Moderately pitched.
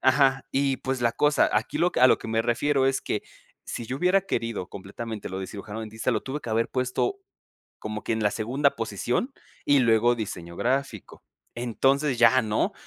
No: low, 120 Hz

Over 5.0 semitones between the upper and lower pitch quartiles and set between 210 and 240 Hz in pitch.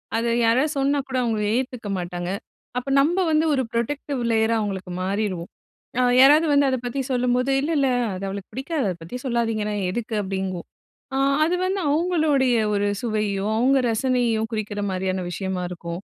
Yes: wide, 5.4 semitones; high, 230 Hz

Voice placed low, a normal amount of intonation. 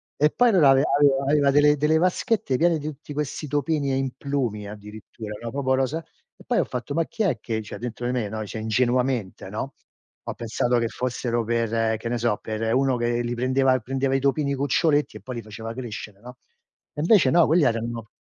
Yes: low, 130 Hz; average, 3.8 semitones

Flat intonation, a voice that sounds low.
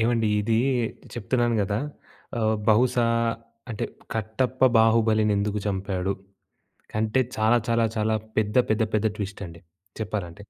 Yes: narrow, 1.9 semitones; low, 110 Hz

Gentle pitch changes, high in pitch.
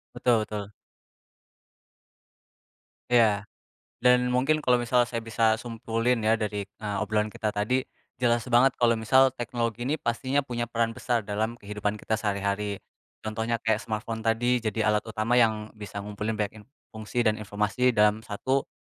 No: narrow, 2.2 semitones; low, 110 Hz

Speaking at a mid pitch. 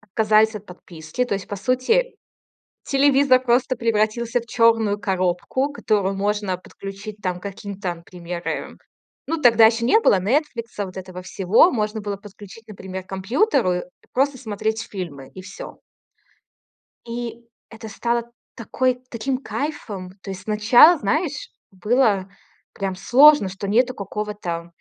No: high, 215 Hz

